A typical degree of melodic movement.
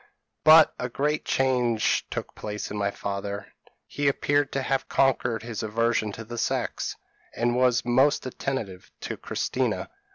Yes: average, 3.7 semitones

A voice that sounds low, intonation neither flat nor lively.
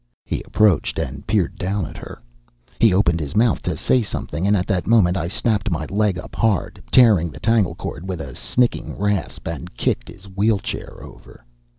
Yes: very low, 95 Hz; average, 4.0 semitones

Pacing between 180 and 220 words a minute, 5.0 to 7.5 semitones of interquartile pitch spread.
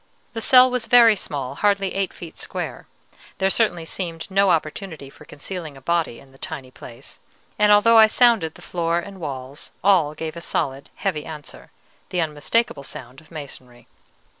No: average, 170 wpm; wide, 5.4 semitones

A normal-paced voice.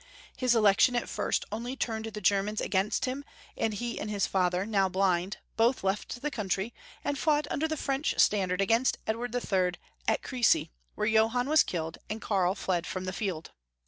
Yes: average, 180 wpm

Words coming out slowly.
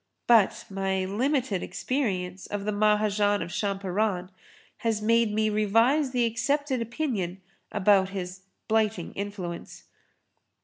Yes: slow, 115 wpm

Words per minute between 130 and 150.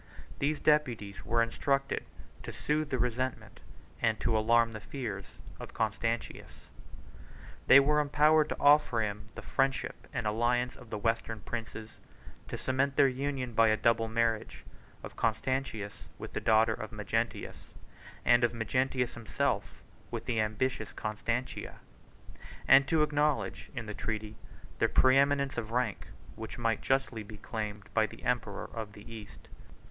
Yes: average, 145 wpm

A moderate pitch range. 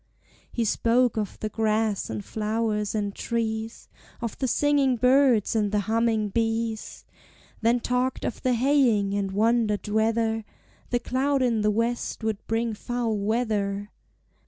No: narrow, 2.2 semitones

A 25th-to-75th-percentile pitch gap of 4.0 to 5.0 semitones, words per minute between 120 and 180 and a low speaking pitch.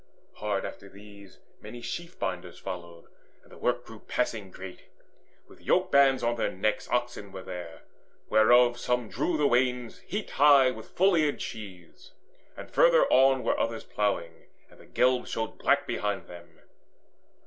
Yes: average, 4.7 semitones; average, 160 wpm; low, 115 Hz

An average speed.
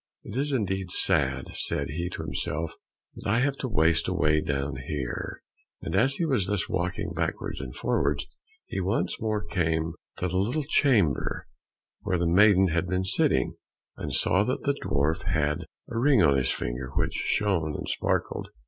Yes: average, 175 wpm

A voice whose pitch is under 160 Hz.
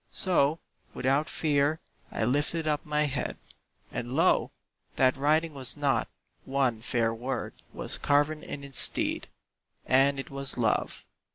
Yes: medium, 140 Hz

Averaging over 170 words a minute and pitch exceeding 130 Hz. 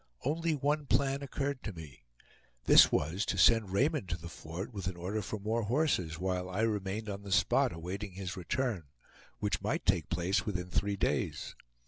No: average, 180 wpm; low, 100 Hz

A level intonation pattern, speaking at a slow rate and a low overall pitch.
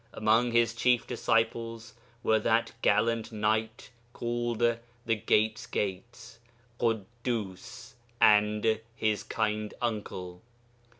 Yes: narrow, 1.6 semitones; slow, 95 wpm; low, 115 Hz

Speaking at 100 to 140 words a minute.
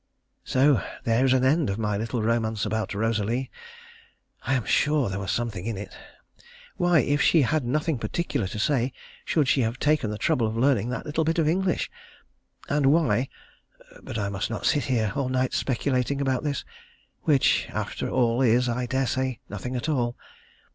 No: average, 180 wpm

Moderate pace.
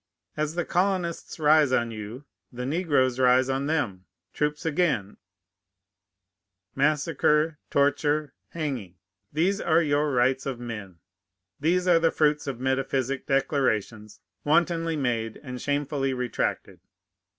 No: slow, 115 wpm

